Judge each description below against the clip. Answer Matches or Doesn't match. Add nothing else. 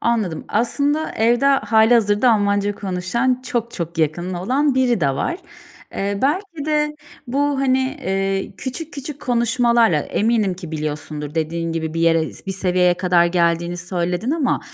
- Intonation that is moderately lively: Doesn't match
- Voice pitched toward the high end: Matches